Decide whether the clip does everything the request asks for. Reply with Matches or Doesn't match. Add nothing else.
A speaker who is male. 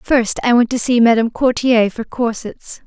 Doesn't match